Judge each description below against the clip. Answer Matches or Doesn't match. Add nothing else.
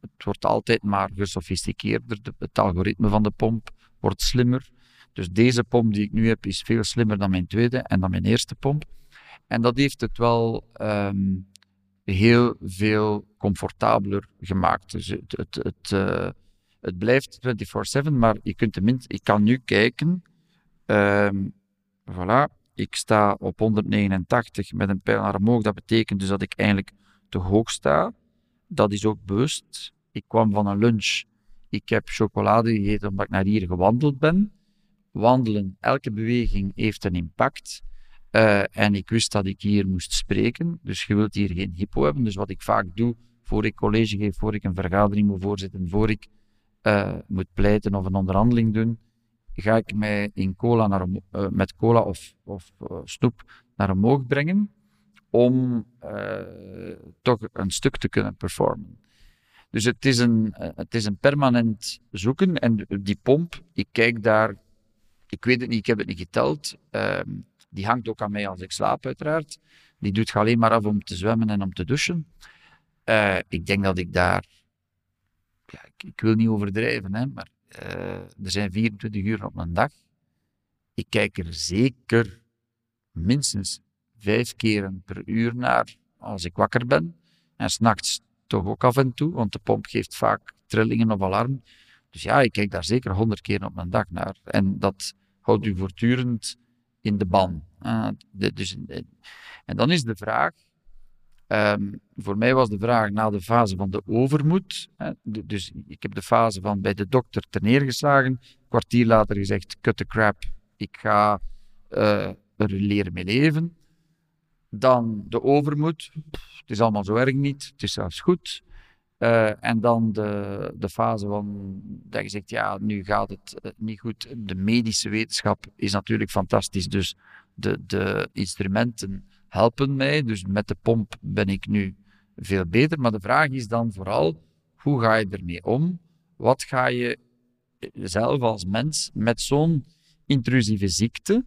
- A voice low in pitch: Matches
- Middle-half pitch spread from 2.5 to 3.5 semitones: Matches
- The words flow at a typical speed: Matches